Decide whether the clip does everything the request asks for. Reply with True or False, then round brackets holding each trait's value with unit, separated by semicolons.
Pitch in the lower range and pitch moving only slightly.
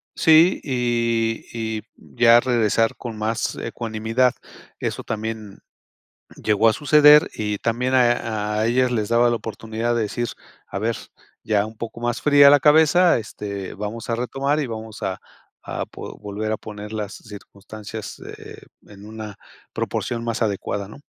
True (115 Hz; 2.2 semitones)